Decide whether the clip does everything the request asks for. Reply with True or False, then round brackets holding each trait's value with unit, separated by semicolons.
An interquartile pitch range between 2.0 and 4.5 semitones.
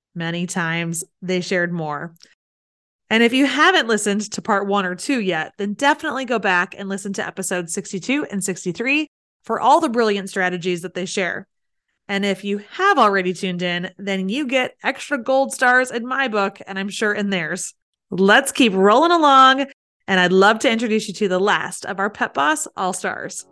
False (5.2 semitones)